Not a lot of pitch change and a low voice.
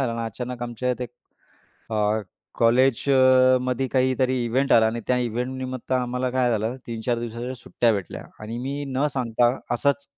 Yes: narrow, 1.7 semitones; low, 125 Hz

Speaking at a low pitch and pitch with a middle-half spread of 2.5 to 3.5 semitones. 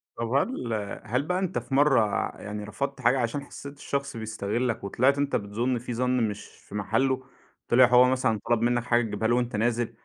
Yes: low, 120 Hz; average, 2.9 semitones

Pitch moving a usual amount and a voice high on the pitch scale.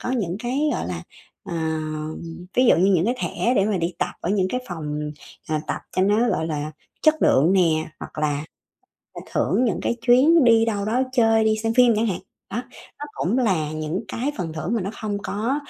No: wide, 6.1 semitones; high, 205 Hz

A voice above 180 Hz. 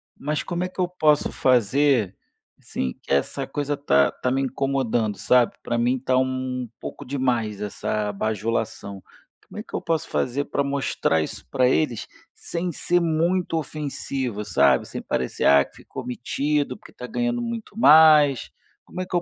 No: low, 135 Hz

